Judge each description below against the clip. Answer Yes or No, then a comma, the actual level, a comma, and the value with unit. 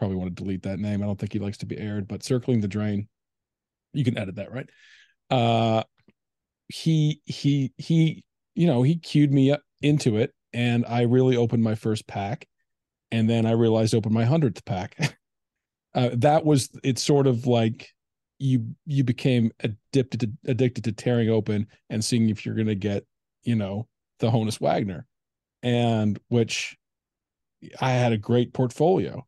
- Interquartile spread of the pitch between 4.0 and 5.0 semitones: No, average, 3.5 semitones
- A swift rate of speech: No, average, 170 wpm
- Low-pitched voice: Yes, low, 120 Hz